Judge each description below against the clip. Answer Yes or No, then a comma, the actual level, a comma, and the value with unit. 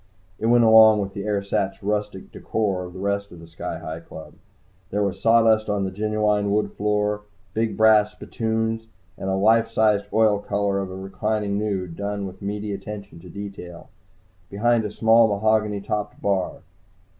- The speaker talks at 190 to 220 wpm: No, average, 170 wpm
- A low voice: Yes, low, 105 Hz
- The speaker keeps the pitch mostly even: Yes, narrow, 1.8 semitones